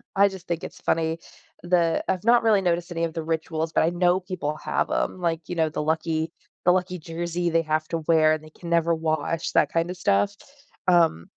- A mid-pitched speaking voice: Yes, medium, 170 Hz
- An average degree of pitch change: No, narrow, 1.9 semitones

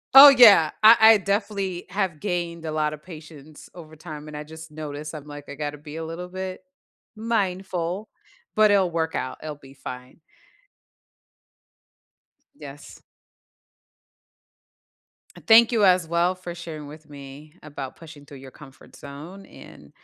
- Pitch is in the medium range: Yes, medium, 160 Hz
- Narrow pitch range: No, average, 4.0 semitones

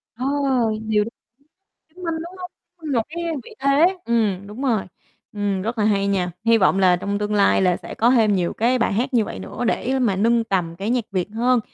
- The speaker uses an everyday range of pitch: Yes, average, 4.2 semitones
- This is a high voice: Yes, high, 225 Hz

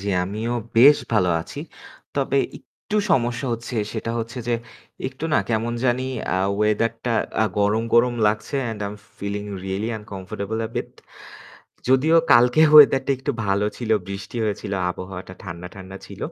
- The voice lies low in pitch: Yes, low, 110 Hz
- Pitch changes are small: No, average, 3.4 semitones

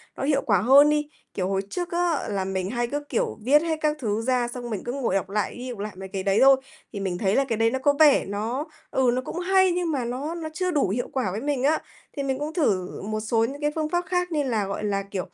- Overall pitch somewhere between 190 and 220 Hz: No, very high, 255 Hz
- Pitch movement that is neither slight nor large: No, wide, 6.3 semitones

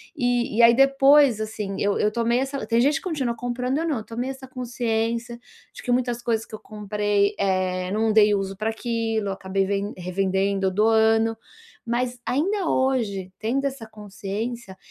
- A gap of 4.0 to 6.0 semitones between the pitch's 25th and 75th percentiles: No, average, 3.3 semitones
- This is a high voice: Yes, high, 225 Hz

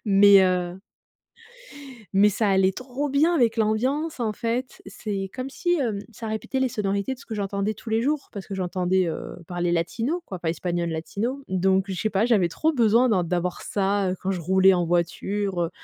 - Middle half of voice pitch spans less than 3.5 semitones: No, average, 4.3 semitones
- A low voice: No, high, 200 Hz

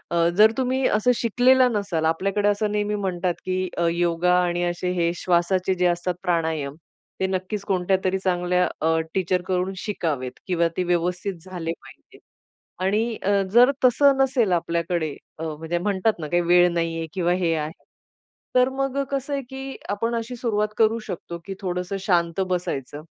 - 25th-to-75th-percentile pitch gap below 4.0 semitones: Yes, average, 3.6 semitones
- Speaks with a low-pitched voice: No, medium, 185 Hz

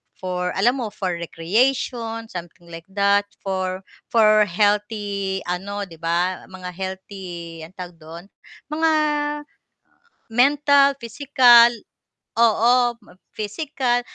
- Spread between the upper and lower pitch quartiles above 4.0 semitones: Yes, average, 4.7 semitones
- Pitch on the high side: Yes, high, 200 Hz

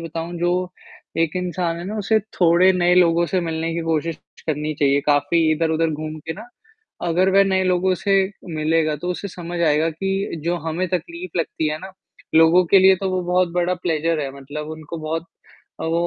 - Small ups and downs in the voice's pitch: Yes, narrow, 2.3 semitones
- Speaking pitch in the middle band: Yes, medium, 170 Hz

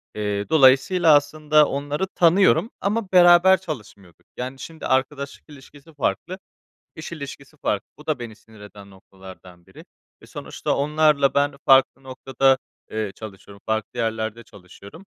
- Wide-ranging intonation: Yes, wide, 6.1 semitones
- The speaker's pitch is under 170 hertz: Yes, low, 135 Hz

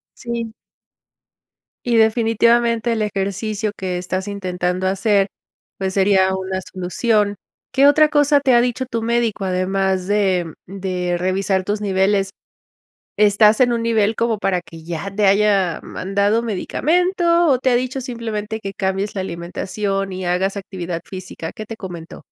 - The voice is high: Yes, high, 200 Hz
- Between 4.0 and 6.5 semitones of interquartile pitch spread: No, average, 3.4 semitones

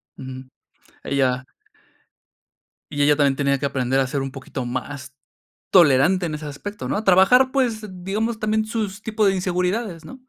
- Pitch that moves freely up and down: Yes, wide, 7.7 semitones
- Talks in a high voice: No, medium, 170 Hz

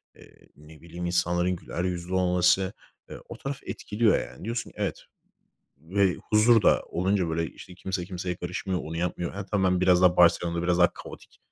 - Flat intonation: Yes, narrow, 1.6 semitones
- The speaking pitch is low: Yes, very low, 90 Hz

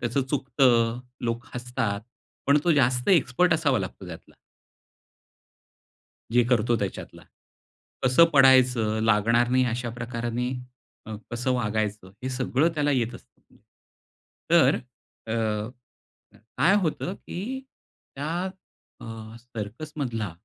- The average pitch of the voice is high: No, low, 125 Hz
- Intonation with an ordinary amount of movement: Yes, average, 3.0 semitones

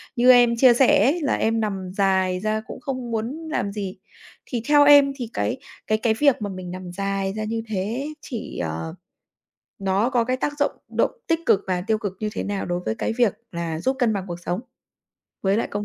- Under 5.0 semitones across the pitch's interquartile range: Yes, average, 4.5 semitones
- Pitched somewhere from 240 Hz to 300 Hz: No, high, 215 Hz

